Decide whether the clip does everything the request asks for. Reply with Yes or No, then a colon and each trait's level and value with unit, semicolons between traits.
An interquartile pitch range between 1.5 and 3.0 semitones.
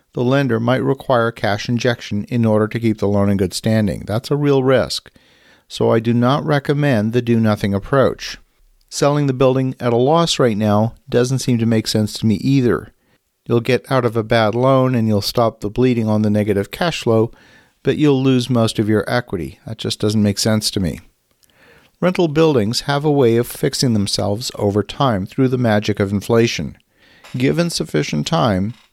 No: average, 3.8 semitones